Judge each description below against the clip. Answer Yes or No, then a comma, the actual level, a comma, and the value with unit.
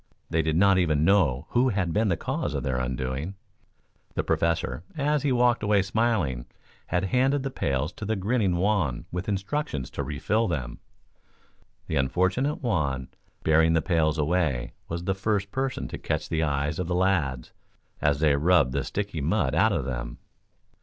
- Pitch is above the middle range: No, very low, 85 Hz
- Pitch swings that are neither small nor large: No, wide, 6.1 semitones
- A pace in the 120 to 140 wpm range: No, average, 175 wpm